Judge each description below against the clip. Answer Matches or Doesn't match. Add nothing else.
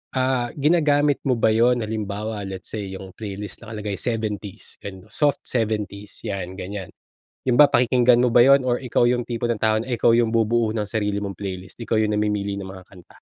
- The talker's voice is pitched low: Matches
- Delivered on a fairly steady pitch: Doesn't match